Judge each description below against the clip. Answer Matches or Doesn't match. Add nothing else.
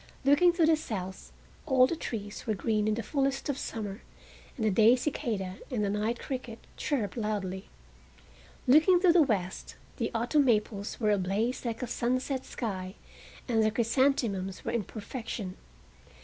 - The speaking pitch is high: Matches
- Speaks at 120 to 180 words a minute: Matches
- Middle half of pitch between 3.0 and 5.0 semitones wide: Matches